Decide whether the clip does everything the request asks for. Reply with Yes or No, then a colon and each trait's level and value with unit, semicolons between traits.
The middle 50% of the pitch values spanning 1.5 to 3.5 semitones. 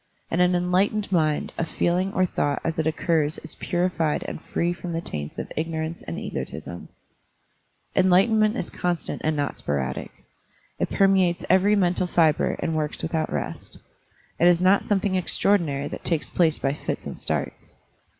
Yes: average, 2.8 semitones